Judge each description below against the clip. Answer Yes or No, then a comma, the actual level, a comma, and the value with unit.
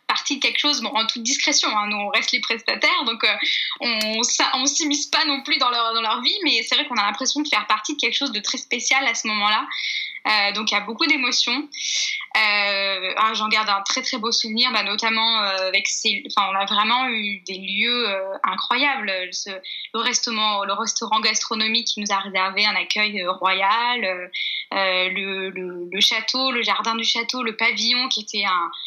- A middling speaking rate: Yes, average, 210 wpm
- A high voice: Yes, high, 225 Hz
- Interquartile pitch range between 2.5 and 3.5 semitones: No, average, 4.0 semitones